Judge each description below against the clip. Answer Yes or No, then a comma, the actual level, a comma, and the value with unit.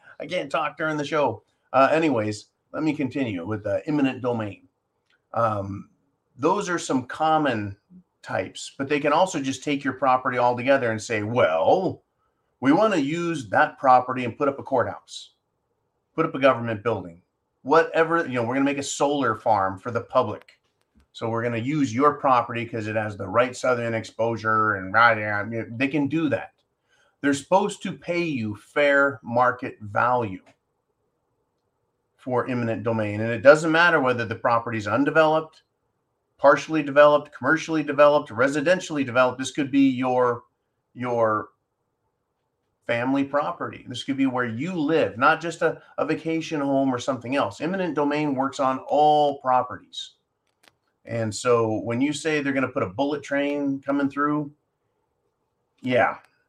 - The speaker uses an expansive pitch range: No, average, 4.1 semitones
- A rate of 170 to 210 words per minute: No, average, 160 wpm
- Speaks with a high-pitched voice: No, low, 135 Hz